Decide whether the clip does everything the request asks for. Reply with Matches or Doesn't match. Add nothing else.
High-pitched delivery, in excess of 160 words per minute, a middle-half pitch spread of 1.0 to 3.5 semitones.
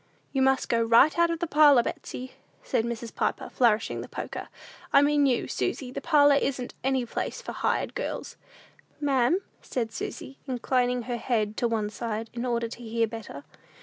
Matches